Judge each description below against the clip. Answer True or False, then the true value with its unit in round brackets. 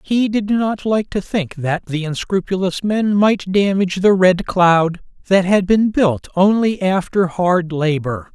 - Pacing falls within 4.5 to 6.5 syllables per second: False (4.0 syllables/s)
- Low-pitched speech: False (185 Hz)